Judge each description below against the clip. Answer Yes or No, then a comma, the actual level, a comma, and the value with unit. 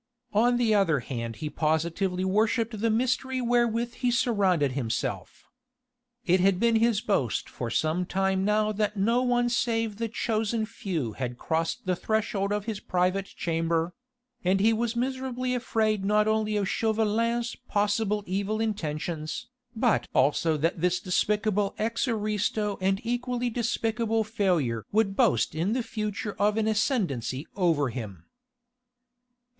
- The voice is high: Yes, high, 210 Hz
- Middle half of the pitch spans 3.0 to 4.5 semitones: Yes, average, 4.2 semitones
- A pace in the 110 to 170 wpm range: Yes, average, 140 wpm